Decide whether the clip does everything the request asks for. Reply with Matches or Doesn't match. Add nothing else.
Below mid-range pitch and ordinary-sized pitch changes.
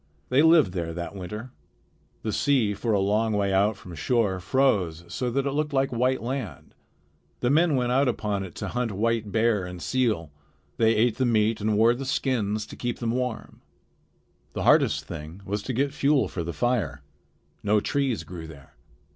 Matches